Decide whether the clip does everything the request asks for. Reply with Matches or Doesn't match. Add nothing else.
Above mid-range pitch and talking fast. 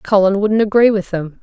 Matches